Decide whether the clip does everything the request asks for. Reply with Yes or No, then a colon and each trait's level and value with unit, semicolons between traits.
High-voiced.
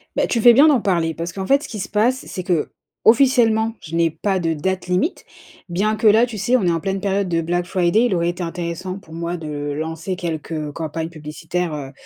No: medium, 180 Hz